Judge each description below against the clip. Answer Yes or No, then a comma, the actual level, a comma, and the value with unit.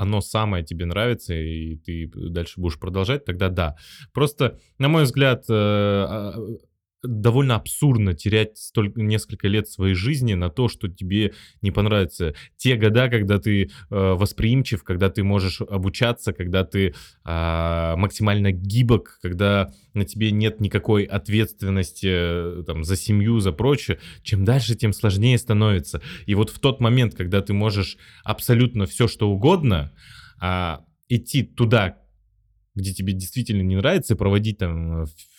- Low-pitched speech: Yes, low, 100 Hz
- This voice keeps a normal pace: Yes, average, 140 wpm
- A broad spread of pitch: No, average, 3.3 semitones